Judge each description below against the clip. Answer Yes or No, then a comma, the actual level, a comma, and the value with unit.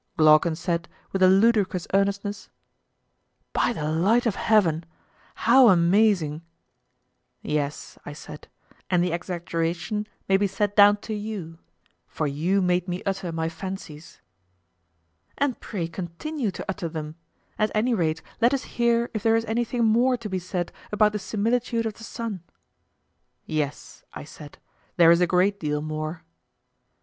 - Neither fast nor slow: Yes, average, 150 wpm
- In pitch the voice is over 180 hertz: Yes, high, 190 Hz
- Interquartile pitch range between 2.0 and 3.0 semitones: No, average, 4.7 semitones